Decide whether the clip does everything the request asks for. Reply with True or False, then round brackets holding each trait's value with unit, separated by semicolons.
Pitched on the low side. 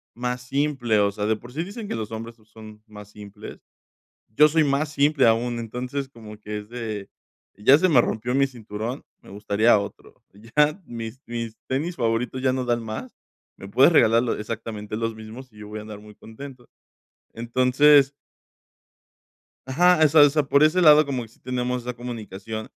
True (120 Hz)